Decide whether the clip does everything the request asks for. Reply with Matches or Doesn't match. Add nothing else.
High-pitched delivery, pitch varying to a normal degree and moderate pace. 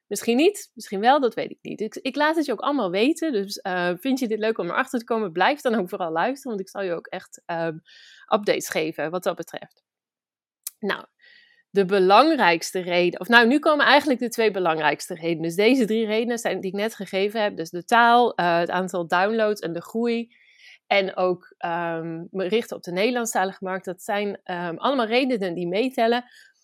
Doesn't match